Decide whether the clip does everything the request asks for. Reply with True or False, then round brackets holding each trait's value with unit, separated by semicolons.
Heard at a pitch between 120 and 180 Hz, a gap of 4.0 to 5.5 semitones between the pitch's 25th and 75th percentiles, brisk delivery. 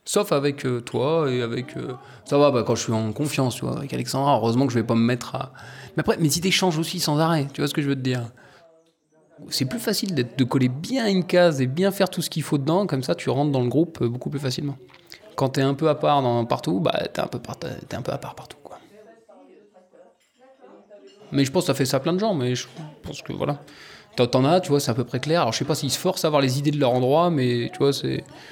True (140 Hz; 4.3 semitones; 280 wpm)